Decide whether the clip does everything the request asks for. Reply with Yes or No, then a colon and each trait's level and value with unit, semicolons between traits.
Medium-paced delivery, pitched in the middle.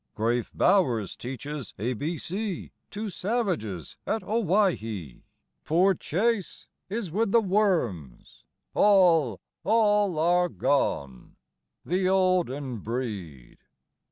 No: slow, 100 wpm; medium, 170 Hz